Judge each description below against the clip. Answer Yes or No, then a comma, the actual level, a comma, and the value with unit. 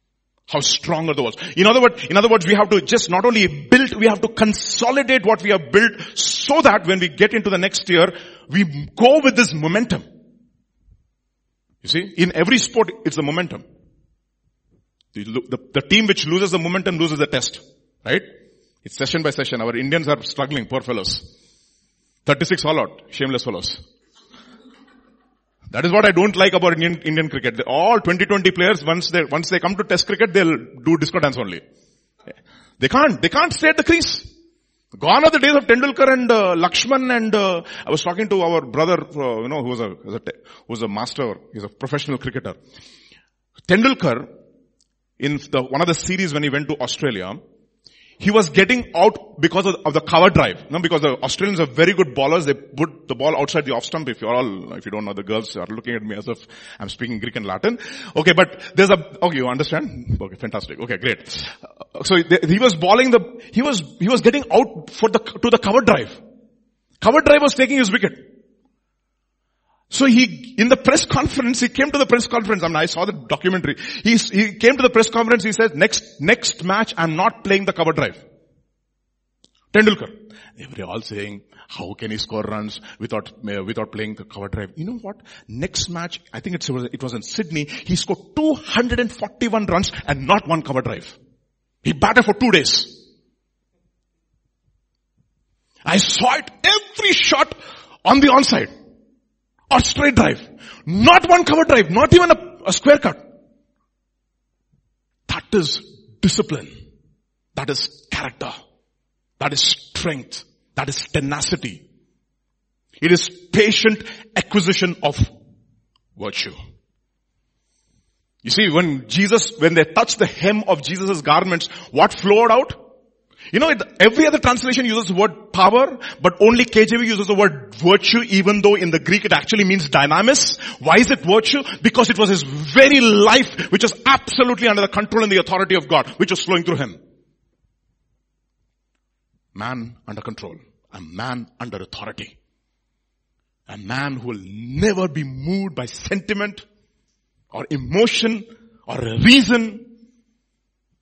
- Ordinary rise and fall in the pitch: No, wide, 7.5 semitones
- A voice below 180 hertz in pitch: No, high, 190 Hz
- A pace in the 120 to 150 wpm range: No, average, 175 wpm